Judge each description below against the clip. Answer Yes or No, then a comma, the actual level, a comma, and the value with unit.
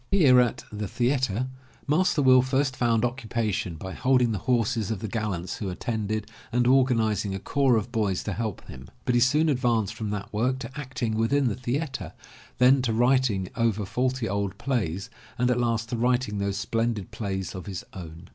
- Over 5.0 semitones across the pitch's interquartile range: No, average, 3.7 semitones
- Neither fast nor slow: Yes, average, 185 wpm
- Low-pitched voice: Yes, low, 115 Hz